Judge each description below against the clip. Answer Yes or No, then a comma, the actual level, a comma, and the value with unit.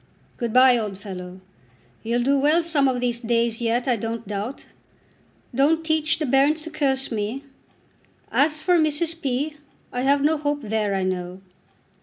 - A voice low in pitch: No, very high, 255 Hz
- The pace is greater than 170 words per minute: No, average, 165 wpm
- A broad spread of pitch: No, average, 5.0 semitones